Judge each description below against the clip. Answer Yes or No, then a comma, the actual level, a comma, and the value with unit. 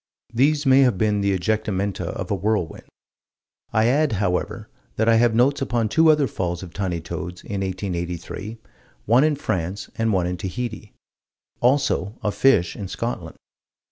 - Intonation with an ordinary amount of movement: Yes, average, 4.8 semitones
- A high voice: No, low, 105 Hz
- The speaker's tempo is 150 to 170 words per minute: Yes, average, 160 wpm